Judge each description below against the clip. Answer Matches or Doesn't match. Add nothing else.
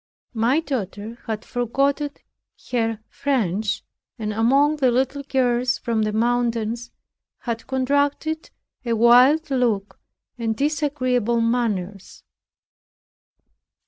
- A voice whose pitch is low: Doesn't match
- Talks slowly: Matches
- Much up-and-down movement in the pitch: Doesn't match